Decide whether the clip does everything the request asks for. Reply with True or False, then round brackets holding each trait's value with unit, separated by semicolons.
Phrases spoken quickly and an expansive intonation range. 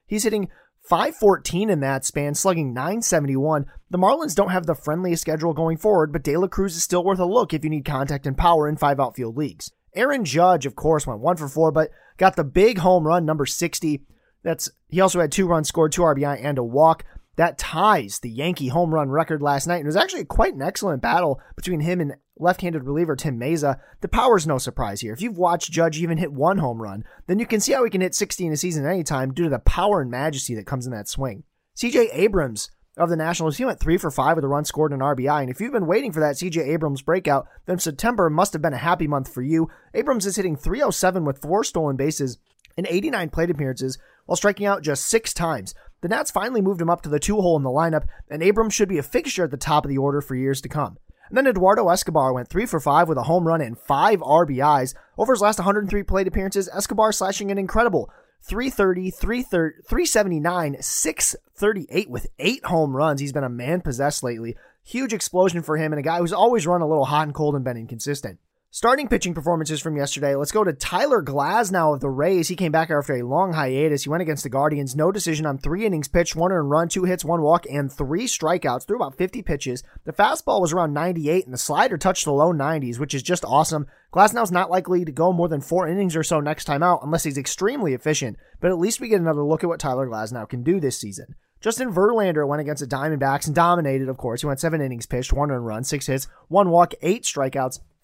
False (235 wpm; 4.3 semitones)